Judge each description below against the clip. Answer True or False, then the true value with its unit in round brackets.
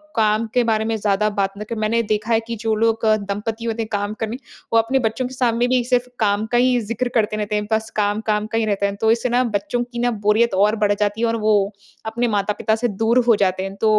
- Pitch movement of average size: False (2.0 semitones)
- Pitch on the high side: True (220 Hz)